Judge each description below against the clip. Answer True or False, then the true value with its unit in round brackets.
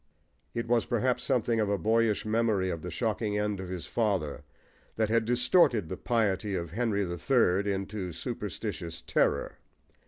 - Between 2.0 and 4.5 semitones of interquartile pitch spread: True (3.7 semitones)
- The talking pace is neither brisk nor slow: True (160 wpm)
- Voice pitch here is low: True (105 Hz)